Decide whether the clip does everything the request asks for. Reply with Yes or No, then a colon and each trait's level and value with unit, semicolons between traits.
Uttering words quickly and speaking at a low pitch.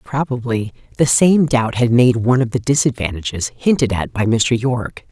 No: average, 175 wpm; low, 120 Hz